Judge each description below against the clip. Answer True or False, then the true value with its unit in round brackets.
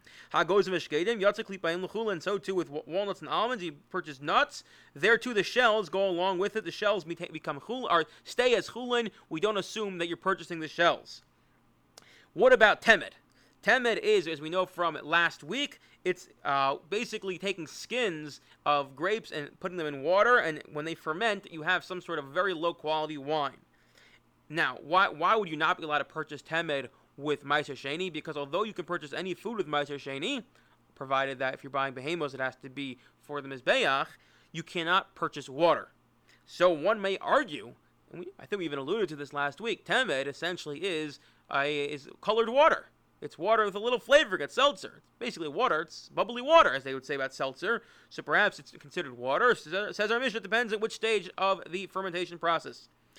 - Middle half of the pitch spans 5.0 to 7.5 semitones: True (5.5 semitones)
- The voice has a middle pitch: True (170 Hz)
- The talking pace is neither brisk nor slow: True (190 wpm)